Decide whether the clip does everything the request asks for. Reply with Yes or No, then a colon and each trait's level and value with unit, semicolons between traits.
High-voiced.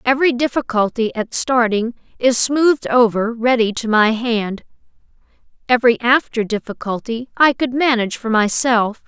Yes: high, 235 Hz